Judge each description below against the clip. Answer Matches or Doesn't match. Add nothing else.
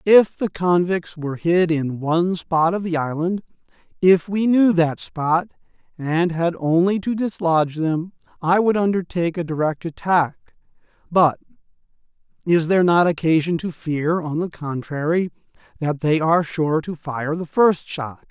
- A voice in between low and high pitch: Matches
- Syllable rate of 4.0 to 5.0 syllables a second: Matches